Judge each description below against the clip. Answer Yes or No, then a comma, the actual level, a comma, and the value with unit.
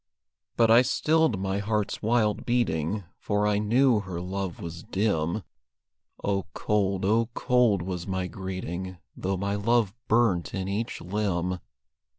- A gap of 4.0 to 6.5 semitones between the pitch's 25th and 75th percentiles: No, average, 3.2 semitones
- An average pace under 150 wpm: Yes, average, 140 wpm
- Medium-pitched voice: No, low, 100 Hz